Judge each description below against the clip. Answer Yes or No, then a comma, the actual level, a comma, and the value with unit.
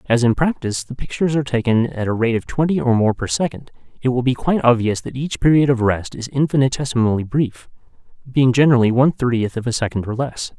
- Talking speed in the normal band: No, fast, 215 wpm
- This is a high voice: No, low, 125 Hz